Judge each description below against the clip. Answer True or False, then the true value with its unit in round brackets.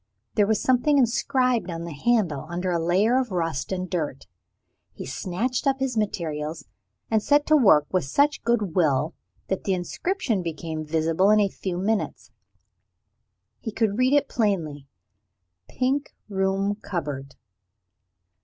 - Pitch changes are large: True (6.4 semitones)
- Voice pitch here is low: False (195 Hz)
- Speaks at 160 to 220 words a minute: False (145 wpm)